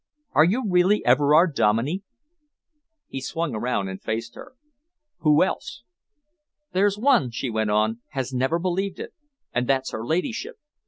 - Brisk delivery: No, average, 145 wpm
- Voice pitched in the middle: Yes, medium, 145 Hz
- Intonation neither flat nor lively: No, wide, 7.7 semitones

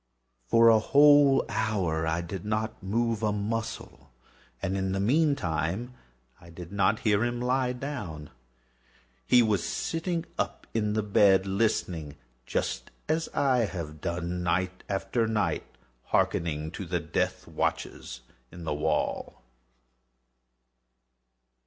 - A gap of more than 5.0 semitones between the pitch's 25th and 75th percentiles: Yes, wide, 5.5 semitones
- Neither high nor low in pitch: No, low, 100 Hz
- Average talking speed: No, slow, 125 wpm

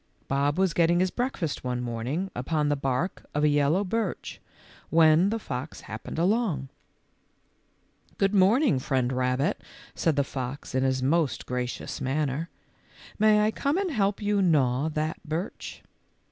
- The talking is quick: No, average, 155 wpm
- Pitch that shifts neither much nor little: No, wide, 6.5 semitones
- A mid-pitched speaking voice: Yes, medium, 155 Hz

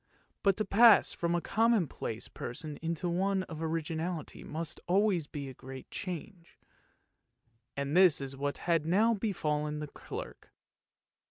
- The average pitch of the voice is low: No, medium, 165 Hz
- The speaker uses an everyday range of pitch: Yes, average, 4.3 semitones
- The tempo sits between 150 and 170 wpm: No, average, 140 wpm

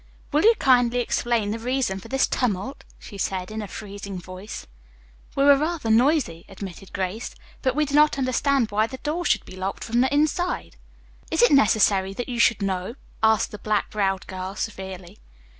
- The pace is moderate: Yes, average, 185 wpm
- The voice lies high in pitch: Yes, high, 220 Hz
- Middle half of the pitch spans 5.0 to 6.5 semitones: Yes, wide, 5.6 semitones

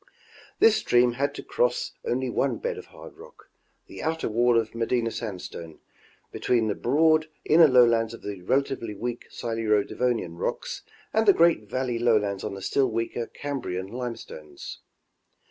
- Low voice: Yes, low, 120 Hz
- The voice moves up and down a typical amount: Yes, average, 4.6 semitones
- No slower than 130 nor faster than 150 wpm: No, average, 160 wpm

